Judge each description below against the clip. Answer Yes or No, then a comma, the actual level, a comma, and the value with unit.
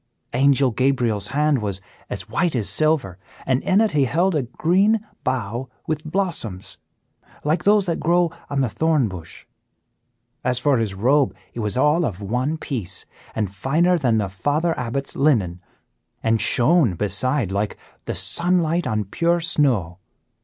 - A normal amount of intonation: No, wide, 7.0 semitones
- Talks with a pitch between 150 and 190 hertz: No, low, 135 Hz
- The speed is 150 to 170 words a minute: Yes, average, 155 wpm